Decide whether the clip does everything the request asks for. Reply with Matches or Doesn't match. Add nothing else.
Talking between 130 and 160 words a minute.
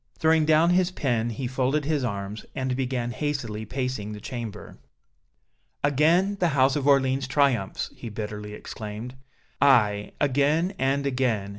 Matches